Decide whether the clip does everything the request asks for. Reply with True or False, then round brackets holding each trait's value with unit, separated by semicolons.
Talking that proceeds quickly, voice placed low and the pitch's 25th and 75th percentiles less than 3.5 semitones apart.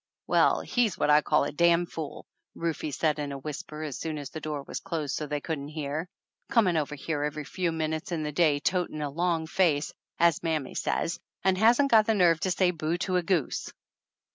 False (215 wpm; 160 Hz; 2.9 semitones)